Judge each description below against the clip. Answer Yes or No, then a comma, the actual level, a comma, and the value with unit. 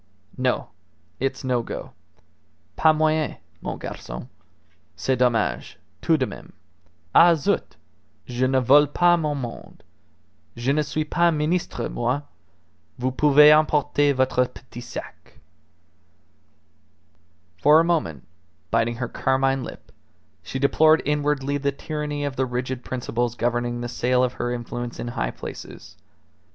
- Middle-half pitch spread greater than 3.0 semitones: Yes, average, 3.5 semitones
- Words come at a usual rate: No, slow, 130 wpm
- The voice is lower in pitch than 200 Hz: Yes, low, 135 Hz